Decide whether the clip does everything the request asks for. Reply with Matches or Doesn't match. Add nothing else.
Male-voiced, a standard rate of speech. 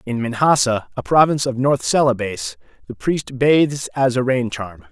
Matches